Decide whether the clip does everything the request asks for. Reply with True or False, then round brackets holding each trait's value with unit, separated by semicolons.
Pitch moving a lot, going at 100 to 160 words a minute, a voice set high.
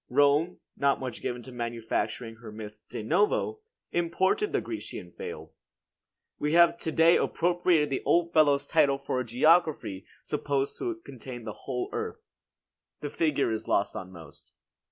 False (6.2 semitones; 155 wpm; 140 Hz)